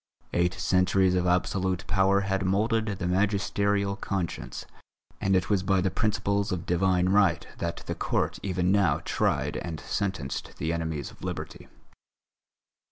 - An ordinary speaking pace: Yes, average, 145 wpm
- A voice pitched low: Yes, very low, 95 Hz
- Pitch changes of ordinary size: No, narrow, 1.9 semitones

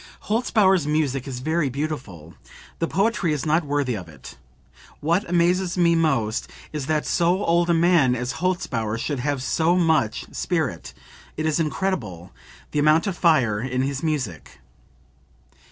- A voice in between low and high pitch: Yes, medium, 155 Hz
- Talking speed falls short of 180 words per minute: Yes, average, 150 wpm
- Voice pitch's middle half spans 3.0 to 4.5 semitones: No, average, 5.1 semitones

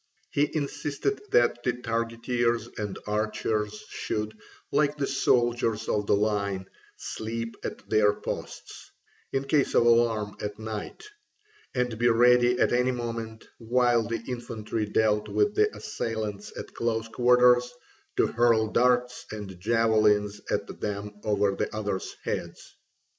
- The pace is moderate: No, slow, 130 wpm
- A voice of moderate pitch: No, low, 115 Hz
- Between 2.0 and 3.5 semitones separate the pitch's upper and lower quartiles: Yes, narrow, 2.5 semitones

